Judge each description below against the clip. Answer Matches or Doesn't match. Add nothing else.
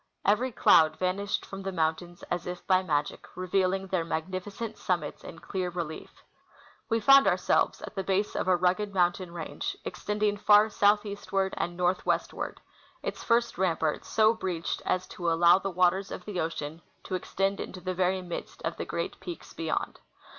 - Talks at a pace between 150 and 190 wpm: Matches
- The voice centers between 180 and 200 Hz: Matches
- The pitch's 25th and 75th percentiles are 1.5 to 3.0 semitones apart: Matches